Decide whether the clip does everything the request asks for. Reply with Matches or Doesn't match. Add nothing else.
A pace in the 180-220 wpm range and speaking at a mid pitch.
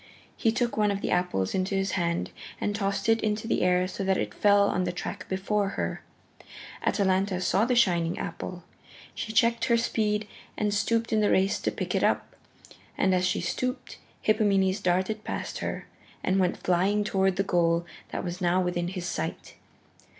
Doesn't match